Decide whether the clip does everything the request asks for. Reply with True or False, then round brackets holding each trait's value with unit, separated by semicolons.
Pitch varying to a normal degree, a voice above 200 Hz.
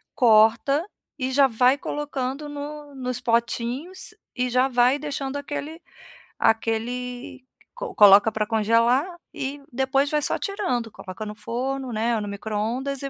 True (3.8 semitones; 255 Hz)